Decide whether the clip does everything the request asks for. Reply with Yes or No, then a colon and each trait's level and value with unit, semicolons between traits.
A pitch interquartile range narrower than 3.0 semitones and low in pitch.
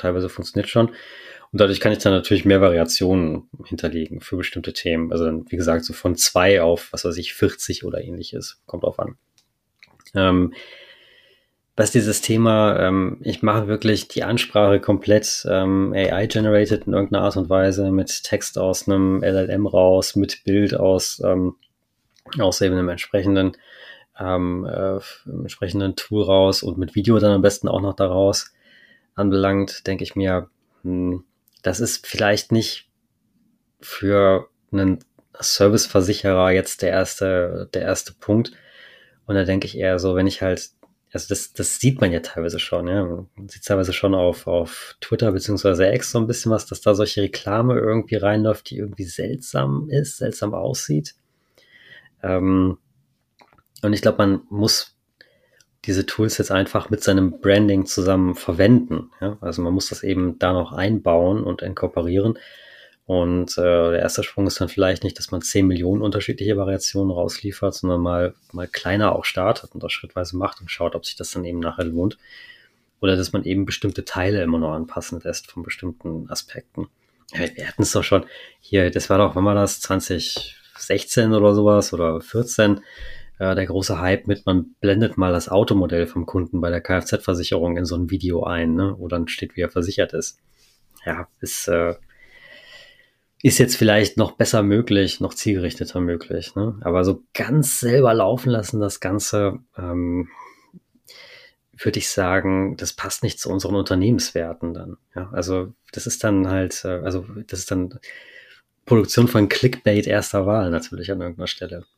Yes: narrow, 2.5 semitones; very low, 95 Hz